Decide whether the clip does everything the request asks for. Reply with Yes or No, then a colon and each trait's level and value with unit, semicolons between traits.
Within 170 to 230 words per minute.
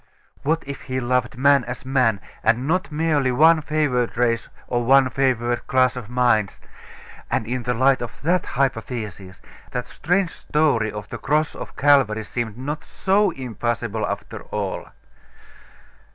No: average, 150 wpm